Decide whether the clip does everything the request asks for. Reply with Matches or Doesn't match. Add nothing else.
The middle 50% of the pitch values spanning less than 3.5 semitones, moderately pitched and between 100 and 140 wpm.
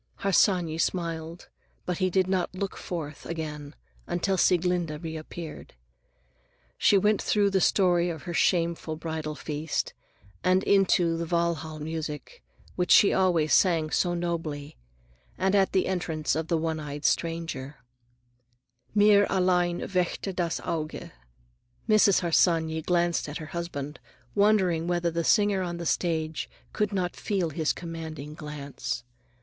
Matches